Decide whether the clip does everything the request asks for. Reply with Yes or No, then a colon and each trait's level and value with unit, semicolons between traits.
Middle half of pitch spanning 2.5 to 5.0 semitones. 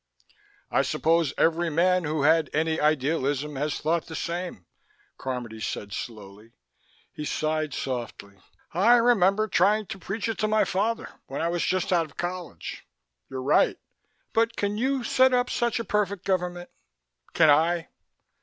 No: wide, 5.4 semitones